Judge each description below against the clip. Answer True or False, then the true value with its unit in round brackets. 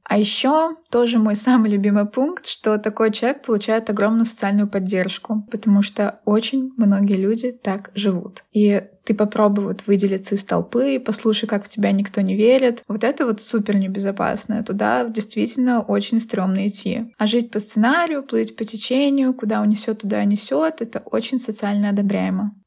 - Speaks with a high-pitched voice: True (215 Hz)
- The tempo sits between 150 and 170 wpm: True (160 wpm)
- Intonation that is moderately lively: False (2.3 semitones)